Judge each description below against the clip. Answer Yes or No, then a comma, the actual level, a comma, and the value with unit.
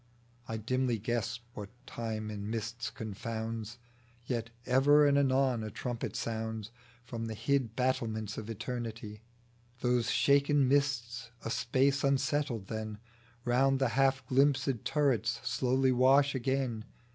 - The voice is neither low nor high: No, low, 120 Hz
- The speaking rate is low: Yes, slow, 125 wpm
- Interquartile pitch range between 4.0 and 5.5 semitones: No, average, 3.2 semitones